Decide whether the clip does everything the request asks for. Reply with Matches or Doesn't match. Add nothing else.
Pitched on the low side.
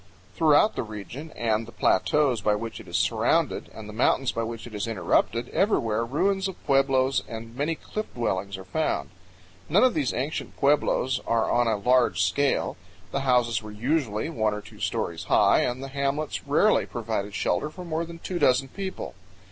Matches